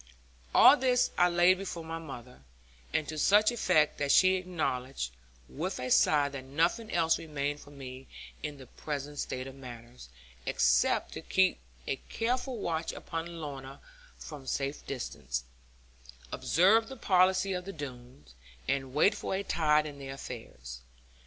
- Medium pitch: Yes, medium, 150 Hz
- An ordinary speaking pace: Yes, average, 150 wpm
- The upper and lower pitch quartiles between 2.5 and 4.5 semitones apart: No, average, 5.3 semitones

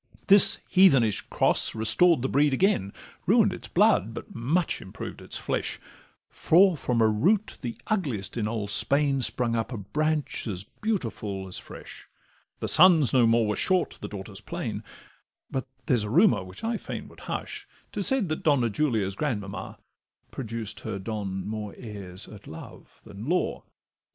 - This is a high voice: No, low, 115 Hz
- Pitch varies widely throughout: Yes, wide, 6.8 semitones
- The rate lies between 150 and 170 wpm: Yes, average, 160 wpm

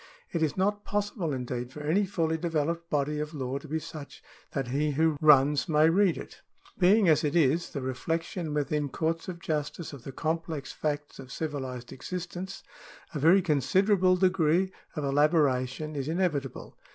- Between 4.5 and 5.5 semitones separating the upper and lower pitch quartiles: No, average, 3.4 semitones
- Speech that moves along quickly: No, average, 165 wpm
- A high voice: No, medium, 155 Hz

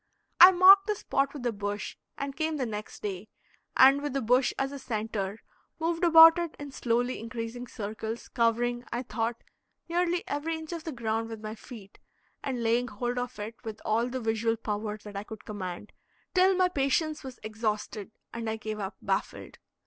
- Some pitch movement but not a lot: Yes, average, 4.7 semitones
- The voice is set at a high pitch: Yes, high, 235 Hz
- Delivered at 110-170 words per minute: No, average, 185 wpm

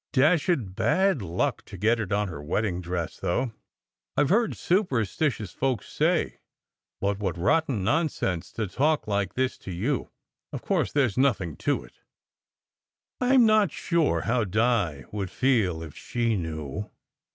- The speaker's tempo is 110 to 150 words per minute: No, average, 160 wpm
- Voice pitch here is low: Yes, low, 110 Hz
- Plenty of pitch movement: Yes, wide, 7.5 semitones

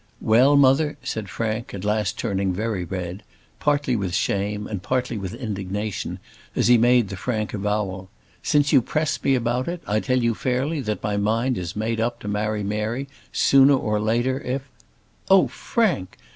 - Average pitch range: Yes, average, 3.9 semitones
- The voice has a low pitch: Yes, low, 110 Hz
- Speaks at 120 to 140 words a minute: No, average, 175 wpm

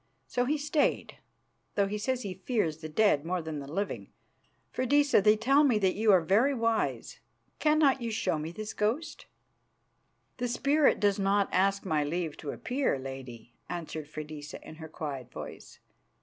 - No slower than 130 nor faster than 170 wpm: Yes, average, 165 wpm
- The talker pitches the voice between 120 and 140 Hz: No, high, 200 Hz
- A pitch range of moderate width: No, wide, 7.7 semitones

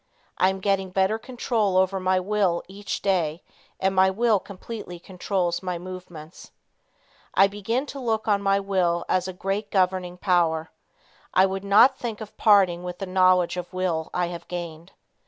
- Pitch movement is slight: Yes, narrow, 2.0 semitones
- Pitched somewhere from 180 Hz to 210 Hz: Yes, high, 190 Hz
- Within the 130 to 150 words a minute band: No, average, 170 wpm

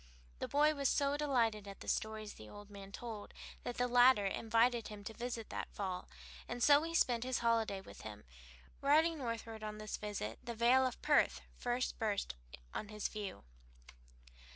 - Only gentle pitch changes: No, average, 3.3 semitones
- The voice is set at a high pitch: Yes, high, 230 Hz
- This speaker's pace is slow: No, average, 180 wpm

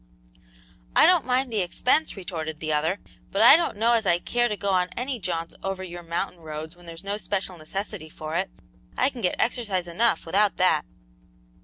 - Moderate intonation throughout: Yes, average, 4.7 semitones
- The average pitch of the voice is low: No, high, 190 Hz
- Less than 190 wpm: No, average, 195 wpm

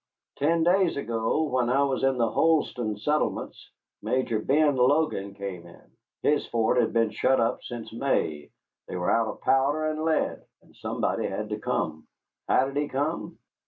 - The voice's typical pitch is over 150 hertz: No, low, 130 Hz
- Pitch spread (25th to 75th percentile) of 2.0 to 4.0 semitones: No, average, 4.8 semitones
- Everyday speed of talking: Yes, average, 170 wpm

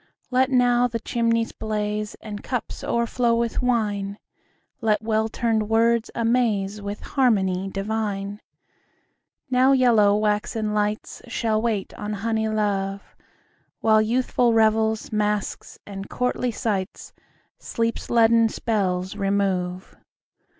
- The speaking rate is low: Yes, slow, 115 wpm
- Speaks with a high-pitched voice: Yes, high, 220 Hz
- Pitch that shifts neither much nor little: No, narrow, 2.1 semitones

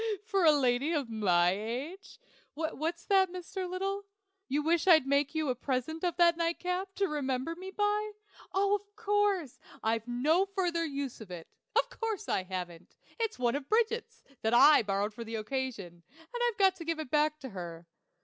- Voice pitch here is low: No, very high, 310 Hz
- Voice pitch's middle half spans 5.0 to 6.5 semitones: No, wide, 7.6 semitones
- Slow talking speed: No, average, 180 wpm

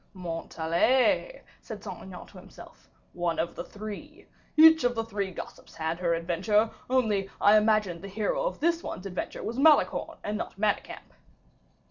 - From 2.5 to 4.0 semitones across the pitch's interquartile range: No, wide, 5.6 semitones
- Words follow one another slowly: No, average, 160 wpm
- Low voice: No, high, 210 Hz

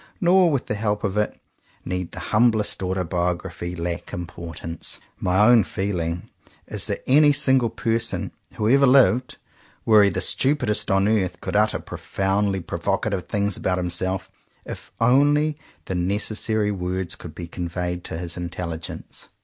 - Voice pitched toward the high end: No, low, 100 Hz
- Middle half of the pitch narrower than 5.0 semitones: Yes, average, 4.3 semitones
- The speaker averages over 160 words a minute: No, average, 150 wpm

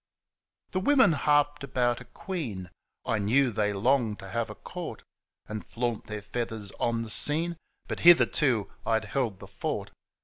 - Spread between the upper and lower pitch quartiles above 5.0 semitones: Yes, wide, 5.4 semitones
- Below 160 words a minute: No, average, 165 wpm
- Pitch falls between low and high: No, low, 120 Hz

